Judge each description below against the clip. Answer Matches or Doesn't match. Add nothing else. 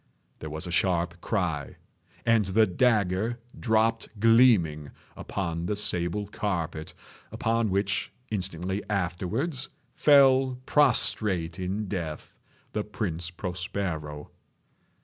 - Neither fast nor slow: Doesn't match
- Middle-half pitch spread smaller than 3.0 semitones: Doesn't match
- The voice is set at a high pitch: Doesn't match